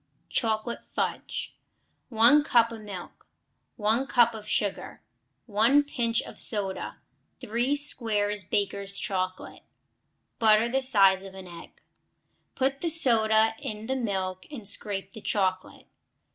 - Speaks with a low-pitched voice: No, high, 220 Hz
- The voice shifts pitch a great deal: No, average, 3.2 semitones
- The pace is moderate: No, slow, 125 wpm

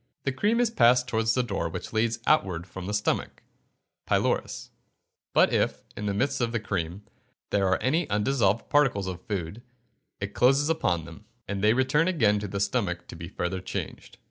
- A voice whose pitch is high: No, low, 105 Hz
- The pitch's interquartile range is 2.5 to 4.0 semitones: No, average, 5.2 semitones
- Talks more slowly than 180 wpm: No, average, 185 wpm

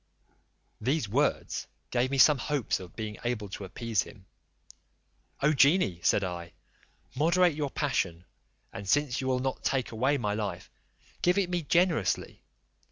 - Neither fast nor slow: Yes, average, 150 wpm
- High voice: No, low, 125 Hz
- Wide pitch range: Yes, wide, 6.2 semitones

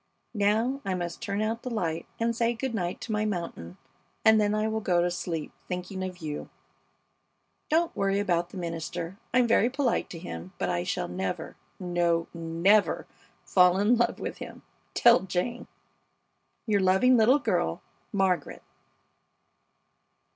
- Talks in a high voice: Yes, high, 195 Hz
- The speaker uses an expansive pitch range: No, average, 4.5 semitones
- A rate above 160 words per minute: No, average, 155 wpm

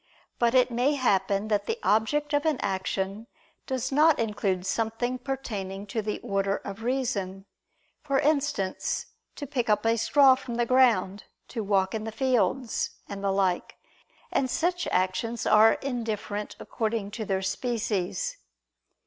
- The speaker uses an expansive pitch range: No, average, 4.7 semitones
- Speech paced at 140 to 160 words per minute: Yes, average, 150 wpm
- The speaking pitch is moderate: No, high, 225 Hz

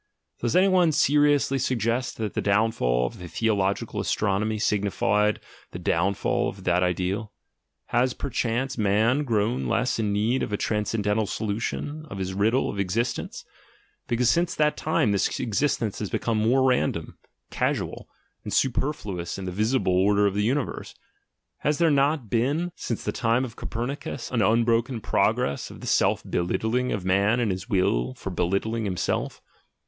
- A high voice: No, low, 110 Hz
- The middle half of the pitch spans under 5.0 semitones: Yes, average, 4.2 semitones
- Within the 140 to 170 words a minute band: Yes, average, 165 wpm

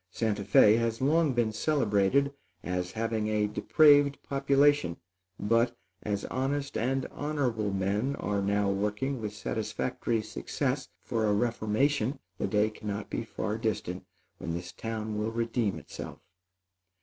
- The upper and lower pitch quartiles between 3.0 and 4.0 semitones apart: No, average, 4.5 semitones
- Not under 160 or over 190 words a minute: No, slow, 135 wpm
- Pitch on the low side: Yes, low, 110 Hz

